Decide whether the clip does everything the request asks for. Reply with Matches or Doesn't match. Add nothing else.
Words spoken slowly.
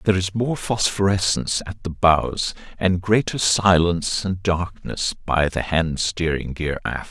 Doesn't match